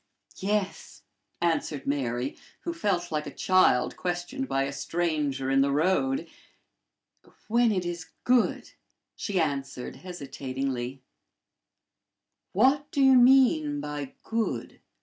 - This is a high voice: No, medium, 175 Hz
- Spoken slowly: Yes, slow, 115 wpm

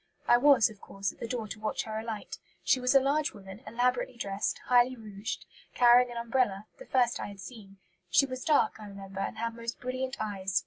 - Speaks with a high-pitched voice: Yes, high, 230 Hz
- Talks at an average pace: No, fast, 215 wpm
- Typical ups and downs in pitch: Yes, average, 3.5 semitones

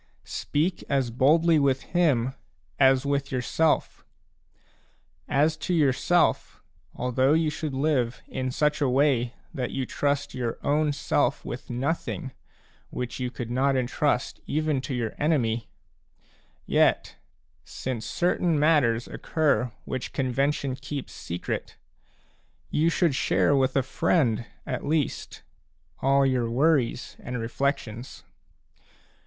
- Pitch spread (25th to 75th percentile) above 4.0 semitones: No, average, 3.1 semitones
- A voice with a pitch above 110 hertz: Yes, low, 135 Hz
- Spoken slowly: Yes, slow, 120 wpm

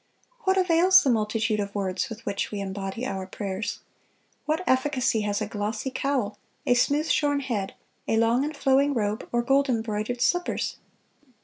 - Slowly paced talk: No, average, 165 wpm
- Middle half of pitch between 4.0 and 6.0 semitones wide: Yes, average, 5.1 semitones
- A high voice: Yes, high, 230 Hz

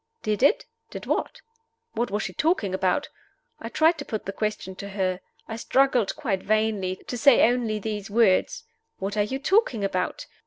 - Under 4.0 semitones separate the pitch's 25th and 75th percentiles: No, average, 4.3 semitones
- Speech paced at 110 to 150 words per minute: No, average, 180 wpm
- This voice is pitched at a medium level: No, high, 215 Hz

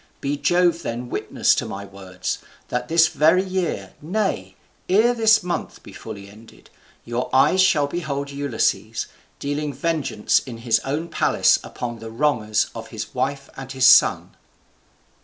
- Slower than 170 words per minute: Yes, average, 150 wpm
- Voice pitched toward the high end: No, medium, 140 Hz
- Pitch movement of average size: No, wide, 6.5 semitones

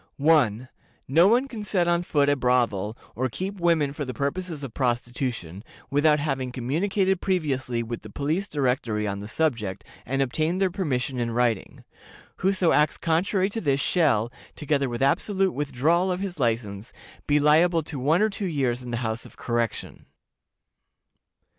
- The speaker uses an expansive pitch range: Yes, wide, 6.1 semitones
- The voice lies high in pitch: No, medium, 140 Hz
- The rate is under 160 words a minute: No, average, 165 wpm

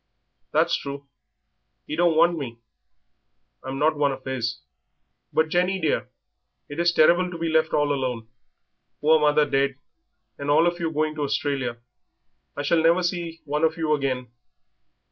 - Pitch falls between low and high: Yes, medium, 150 Hz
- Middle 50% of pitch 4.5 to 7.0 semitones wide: No, average, 3.0 semitones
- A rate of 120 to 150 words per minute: No, average, 160 wpm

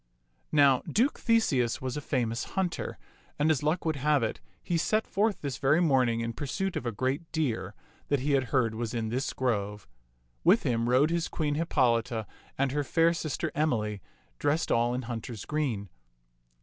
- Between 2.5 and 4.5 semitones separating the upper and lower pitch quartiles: No, average, 4.9 semitones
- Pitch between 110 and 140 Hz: Yes, low, 135 Hz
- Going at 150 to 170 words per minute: No, average, 180 wpm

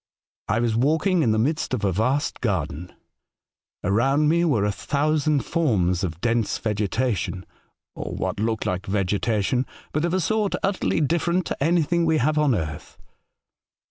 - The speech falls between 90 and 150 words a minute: No, average, 165 wpm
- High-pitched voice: No, low, 125 Hz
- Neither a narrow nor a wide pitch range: No, wide, 7.3 semitones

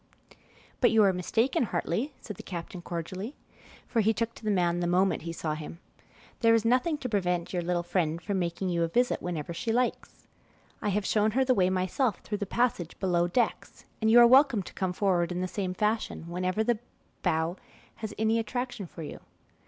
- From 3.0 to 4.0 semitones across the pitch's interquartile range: No, average, 4.6 semitones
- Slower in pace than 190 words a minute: No, fast, 205 wpm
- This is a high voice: Yes, high, 195 Hz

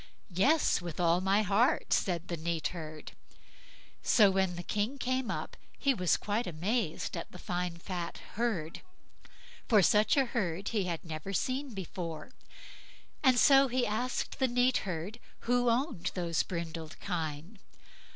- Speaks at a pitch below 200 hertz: Yes, high, 190 Hz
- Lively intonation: Yes, wide, 6.0 semitones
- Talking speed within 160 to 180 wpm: No, average, 150 wpm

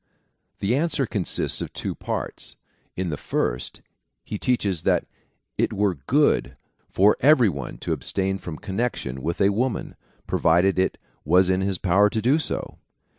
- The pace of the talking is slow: No, average, 155 wpm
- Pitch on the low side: Yes, very low, 95 Hz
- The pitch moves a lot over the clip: No, average, 4.6 semitones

